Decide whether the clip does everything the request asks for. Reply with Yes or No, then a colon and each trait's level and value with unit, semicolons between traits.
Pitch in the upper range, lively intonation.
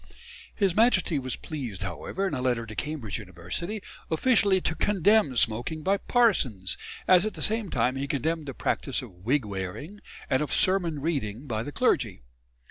No: medium, 150 Hz; wide, 7.7 semitones